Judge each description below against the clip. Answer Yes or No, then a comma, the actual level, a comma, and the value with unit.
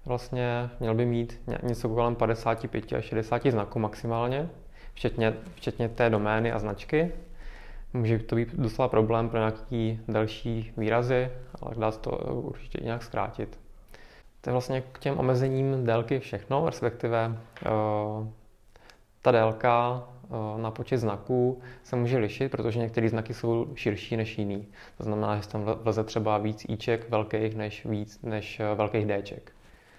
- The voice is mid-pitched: No, low, 115 Hz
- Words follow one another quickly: No, average, 145 wpm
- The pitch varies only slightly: Yes, narrow, 2.1 semitones